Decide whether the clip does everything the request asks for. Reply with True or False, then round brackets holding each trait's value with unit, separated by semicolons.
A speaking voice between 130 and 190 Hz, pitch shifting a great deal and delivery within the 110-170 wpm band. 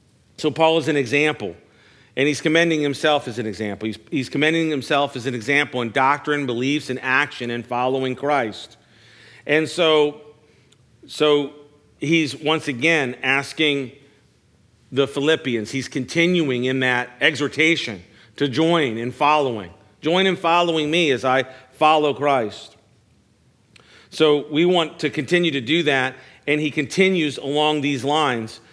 False (140 Hz; 3.5 semitones; 140 wpm)